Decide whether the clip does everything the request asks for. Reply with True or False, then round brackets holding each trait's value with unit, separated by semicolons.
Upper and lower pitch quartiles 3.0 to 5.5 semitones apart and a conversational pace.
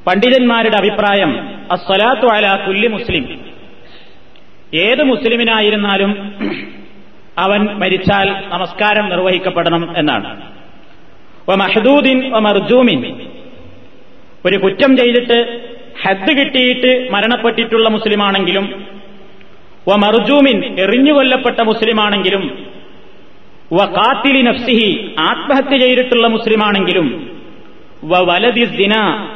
False (3.9 semitones; 55 wpm)